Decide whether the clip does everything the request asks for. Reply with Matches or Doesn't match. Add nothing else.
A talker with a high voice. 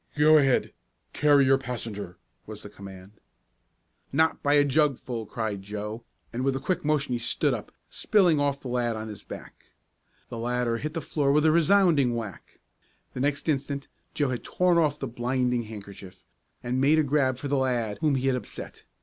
Doesn't match